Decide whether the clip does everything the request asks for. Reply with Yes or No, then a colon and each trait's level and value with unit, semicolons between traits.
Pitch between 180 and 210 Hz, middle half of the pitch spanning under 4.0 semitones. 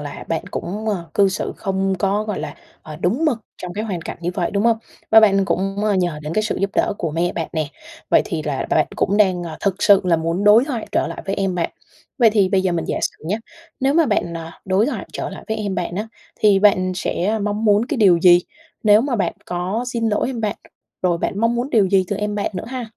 Yes: high, 195 Hz; average, 3.5 semitones